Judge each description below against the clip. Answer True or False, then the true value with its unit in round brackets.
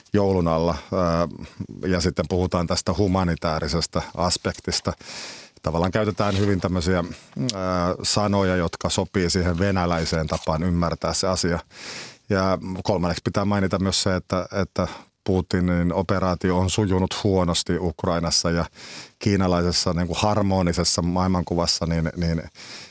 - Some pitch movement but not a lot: False (2.0 semitones)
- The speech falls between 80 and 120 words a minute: True (115 wpm)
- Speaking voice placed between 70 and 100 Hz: True (90 Hz)